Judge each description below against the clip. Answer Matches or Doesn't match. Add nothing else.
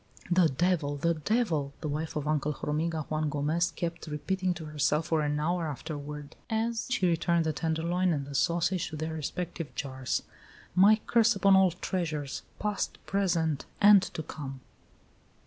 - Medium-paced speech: Matches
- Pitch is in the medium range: Matches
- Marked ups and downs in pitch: Doesn't match